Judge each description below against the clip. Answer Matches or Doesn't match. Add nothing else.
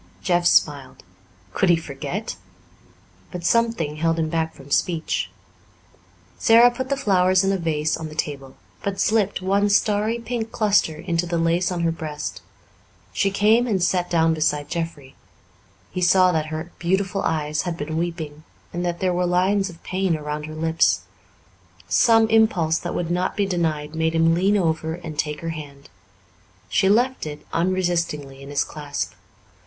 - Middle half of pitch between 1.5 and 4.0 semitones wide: Matches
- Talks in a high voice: Doesn't match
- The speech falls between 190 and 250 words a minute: Doesn't match